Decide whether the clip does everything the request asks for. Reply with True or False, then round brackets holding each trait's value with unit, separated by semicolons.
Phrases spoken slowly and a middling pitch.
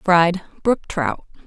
True (125 wpm; 180 Hz)